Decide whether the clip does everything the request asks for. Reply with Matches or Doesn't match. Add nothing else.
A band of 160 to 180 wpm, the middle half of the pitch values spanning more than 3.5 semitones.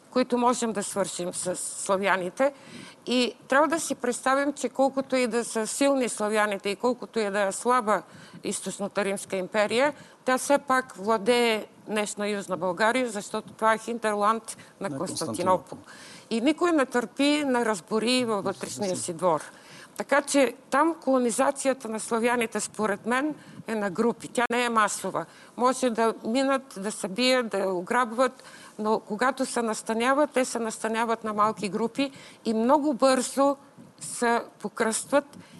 Doesn't match